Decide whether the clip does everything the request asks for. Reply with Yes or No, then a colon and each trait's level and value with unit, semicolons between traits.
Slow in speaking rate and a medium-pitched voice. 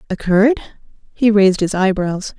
No: slow, 125 wpm; high, 200 Hz